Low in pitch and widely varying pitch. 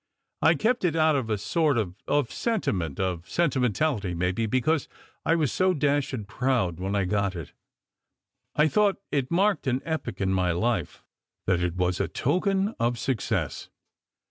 Yes: low, 125 Hz; wide, 8.8 semitones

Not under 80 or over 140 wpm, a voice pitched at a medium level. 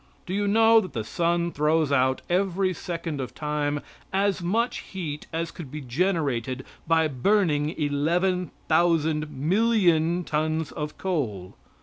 Yes: slow, 135 wpm; medium, 160 Hz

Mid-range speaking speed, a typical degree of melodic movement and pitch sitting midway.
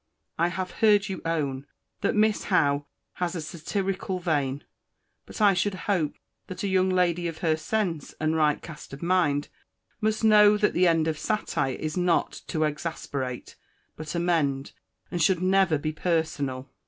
Yes: average, 165 wpm; average, 3.7 semitones; medium, 170 Hz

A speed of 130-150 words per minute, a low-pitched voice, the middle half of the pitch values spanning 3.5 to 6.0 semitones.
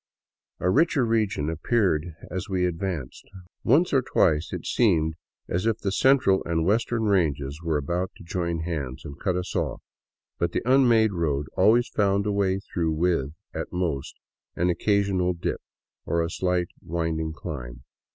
No: average, 165 wpm; very low, 90 Hz; average, 3.9 semitones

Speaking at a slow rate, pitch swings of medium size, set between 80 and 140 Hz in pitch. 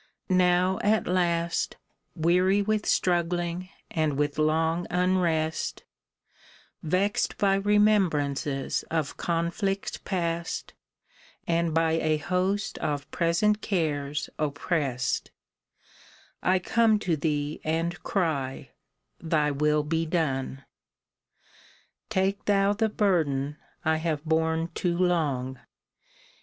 No: slow, 100 wpm; average, 3.2 semitones; medium, 165 Hz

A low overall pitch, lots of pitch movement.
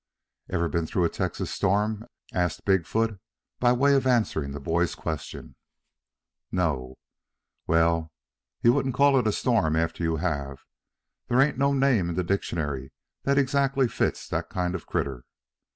Yes: very low, 90 Hz; wide, 7.4 semitones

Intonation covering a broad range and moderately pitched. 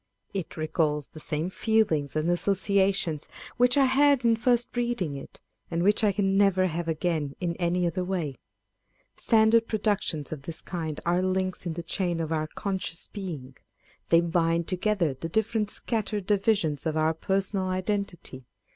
No: average, 4.2 semitones; medium, 180 Hz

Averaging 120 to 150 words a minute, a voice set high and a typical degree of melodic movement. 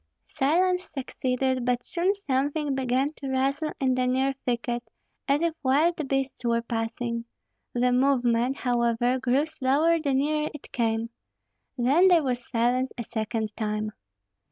Yes: average, 140 wpm; very high, 260 Hz; average, 3.0 semitones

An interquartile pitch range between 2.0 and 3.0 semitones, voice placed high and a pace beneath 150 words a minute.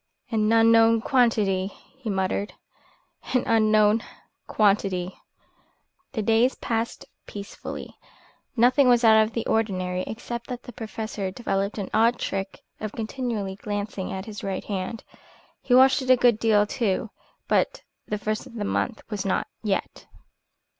Yes: narrow, 2.6 semitones; high, 220 Hz; average, 140 wpm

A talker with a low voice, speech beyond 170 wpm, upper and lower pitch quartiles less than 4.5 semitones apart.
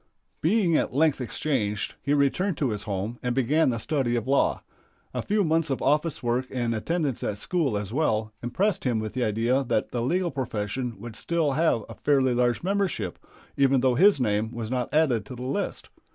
No: low, 130 Hz; average, 195 wpm; average, 5.0 semitones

